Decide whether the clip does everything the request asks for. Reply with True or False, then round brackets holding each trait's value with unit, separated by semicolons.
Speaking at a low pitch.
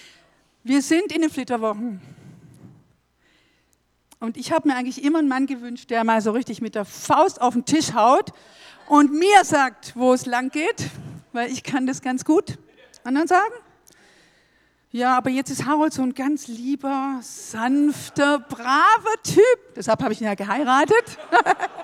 False (265 Hz)